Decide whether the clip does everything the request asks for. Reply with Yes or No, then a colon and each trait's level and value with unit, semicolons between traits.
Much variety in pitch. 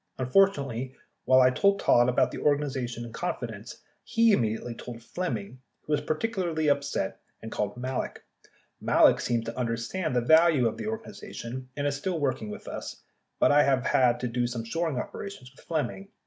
No: average, 4.8 semitones